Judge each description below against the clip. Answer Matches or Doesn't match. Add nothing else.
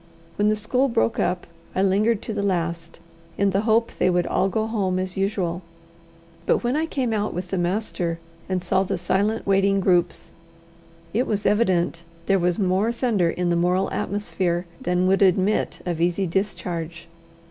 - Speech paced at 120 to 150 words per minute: Doesn't match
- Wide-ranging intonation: Doesn't match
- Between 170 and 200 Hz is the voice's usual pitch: Matches